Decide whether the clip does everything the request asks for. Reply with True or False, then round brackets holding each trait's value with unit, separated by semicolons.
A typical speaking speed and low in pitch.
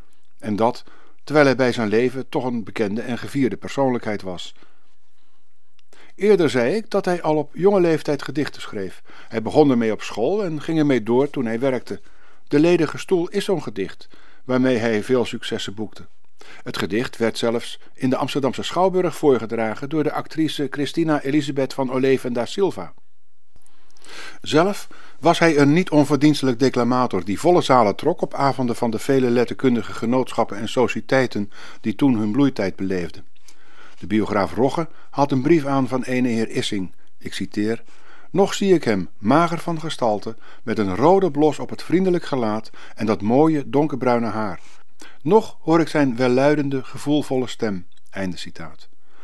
True (160 wpm; 130 Hz)